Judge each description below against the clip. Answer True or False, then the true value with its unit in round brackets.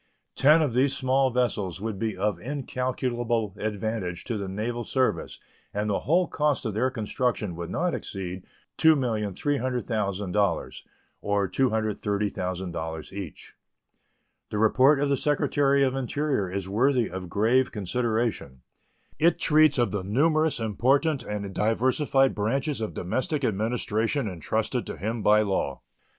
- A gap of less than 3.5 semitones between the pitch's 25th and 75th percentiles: False (4.8 semitones)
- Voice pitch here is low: True (115 Hz)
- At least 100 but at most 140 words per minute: True (135 wpm)